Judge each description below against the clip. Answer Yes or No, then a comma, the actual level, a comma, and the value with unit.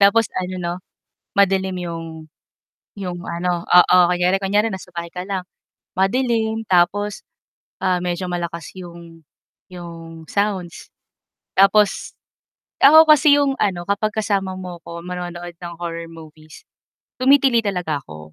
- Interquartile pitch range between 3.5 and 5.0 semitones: No, average, 2.8 semitones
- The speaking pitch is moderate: Yes, medium, 180 Hz